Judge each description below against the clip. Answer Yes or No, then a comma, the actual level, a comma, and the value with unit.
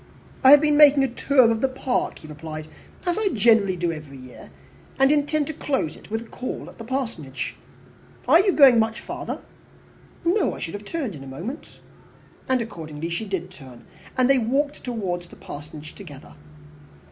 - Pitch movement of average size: No, wide, 8.9 semitones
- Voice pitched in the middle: No, high, 225 Hz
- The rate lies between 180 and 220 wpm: Yes, average, 185 wpm